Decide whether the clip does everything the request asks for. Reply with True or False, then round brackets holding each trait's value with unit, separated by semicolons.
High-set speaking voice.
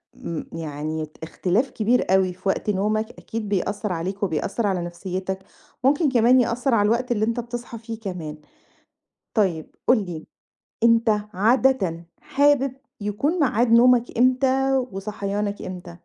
True (210 Hz)